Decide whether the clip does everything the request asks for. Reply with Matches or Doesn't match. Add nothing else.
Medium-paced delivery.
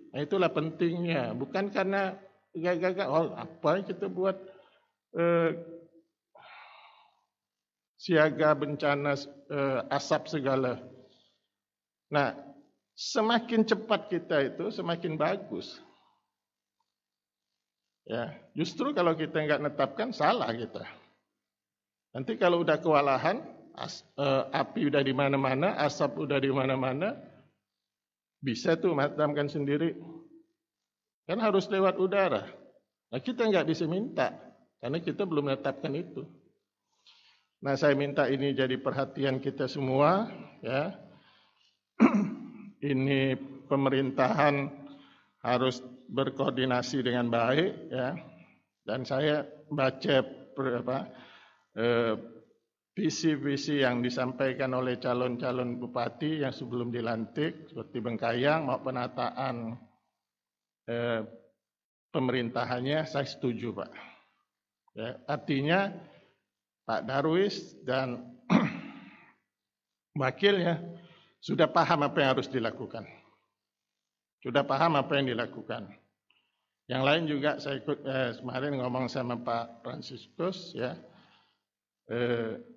Matches